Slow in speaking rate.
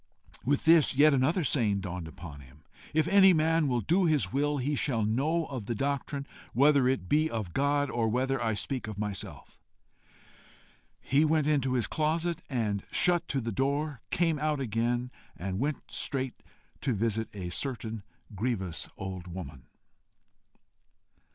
No: average, 155 wpm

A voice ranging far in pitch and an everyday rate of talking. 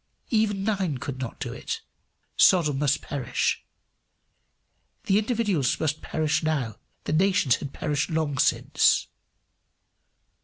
No: wide, 5.7 semitones; slow, 115 wpm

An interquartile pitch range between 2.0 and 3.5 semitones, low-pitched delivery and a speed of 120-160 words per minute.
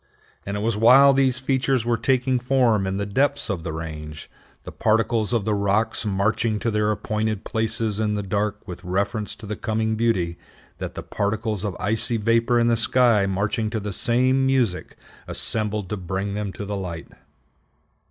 No: average, 2.7 semitones; low, 110 Hz; average, 180 wpm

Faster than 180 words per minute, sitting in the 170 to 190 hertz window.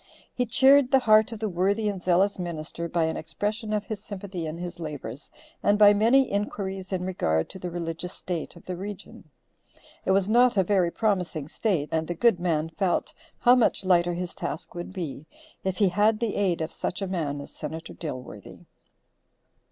Yes: average, 190 wpm; medium, 185 Hz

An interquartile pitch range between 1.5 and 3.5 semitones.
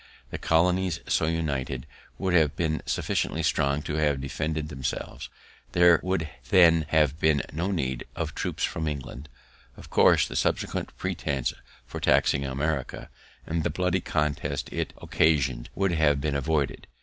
Yes: average, 2.8 semitones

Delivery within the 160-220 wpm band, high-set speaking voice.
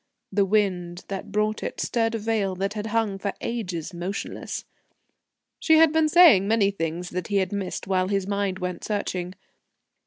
Yes: average, 175 wpm; high, 200 Hz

